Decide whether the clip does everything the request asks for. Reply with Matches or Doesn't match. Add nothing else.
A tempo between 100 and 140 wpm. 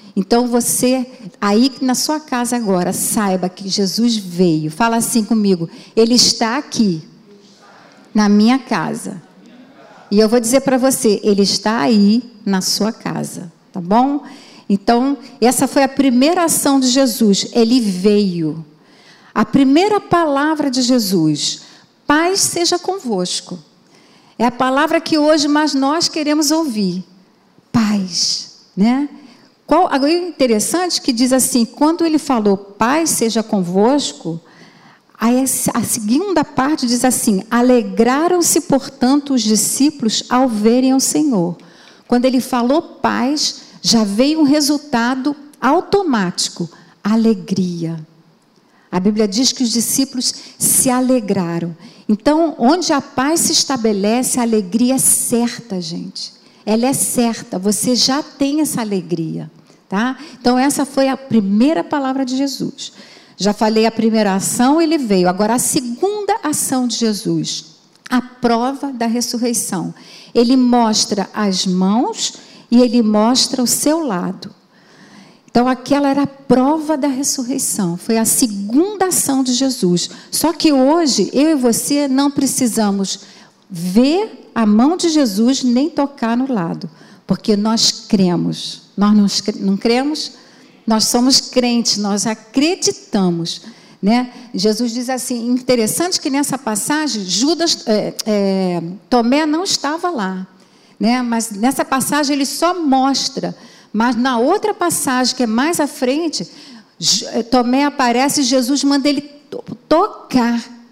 Matches